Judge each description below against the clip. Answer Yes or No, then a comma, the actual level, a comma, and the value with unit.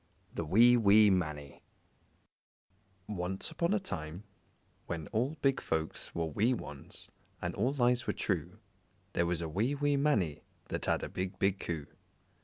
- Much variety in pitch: Yes, wide, 6.8 semitones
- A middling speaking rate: Yes, average, 155 wpm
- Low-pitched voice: Yes, very low, 95 Hz